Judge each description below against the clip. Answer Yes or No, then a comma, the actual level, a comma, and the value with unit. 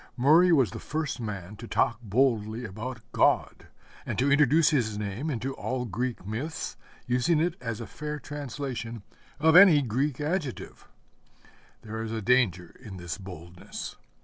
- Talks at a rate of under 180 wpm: Yes, average, 150 wpm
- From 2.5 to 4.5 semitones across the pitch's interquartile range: No, average, 5.2 semitones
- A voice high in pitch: No, low, 125 Hz